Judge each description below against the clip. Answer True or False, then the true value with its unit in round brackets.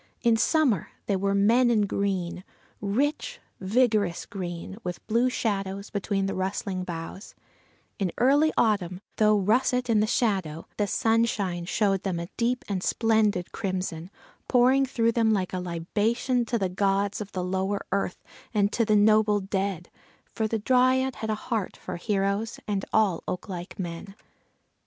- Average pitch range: True (3.3 semitones)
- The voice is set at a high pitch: True (205 Hz)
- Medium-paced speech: True (155 wpm)